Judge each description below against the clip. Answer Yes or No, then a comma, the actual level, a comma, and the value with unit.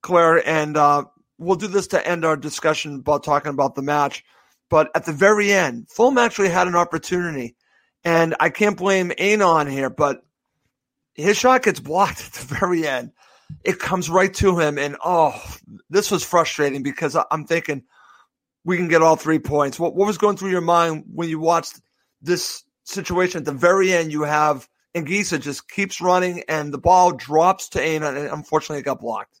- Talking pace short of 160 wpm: No, average, 190 wpm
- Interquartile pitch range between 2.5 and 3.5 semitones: No, average, 4.1 semitones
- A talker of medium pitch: Yes, medium, 165 Hz